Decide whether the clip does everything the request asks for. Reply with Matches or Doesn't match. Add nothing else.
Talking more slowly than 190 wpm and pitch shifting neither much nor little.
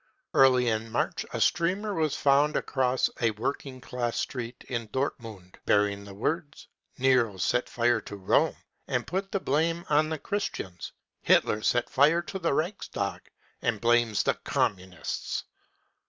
Doesn't match